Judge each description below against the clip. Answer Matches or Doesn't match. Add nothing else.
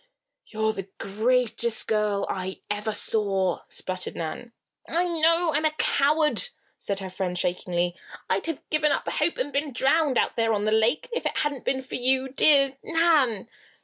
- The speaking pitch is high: Matches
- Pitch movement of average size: Doesn't match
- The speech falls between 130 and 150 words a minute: Doesn't match